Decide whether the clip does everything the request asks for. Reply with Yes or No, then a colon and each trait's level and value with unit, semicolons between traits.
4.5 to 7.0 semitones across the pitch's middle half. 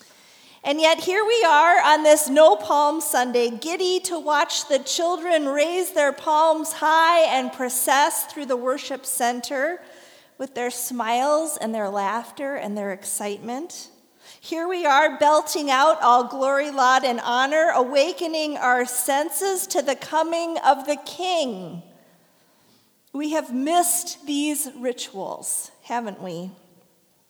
No: average, 4.1 semitones